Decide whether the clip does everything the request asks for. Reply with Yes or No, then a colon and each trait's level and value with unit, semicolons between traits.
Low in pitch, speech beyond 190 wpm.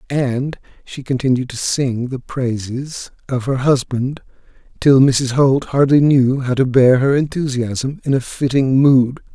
No: low, 130 Hz; average, 155 wpm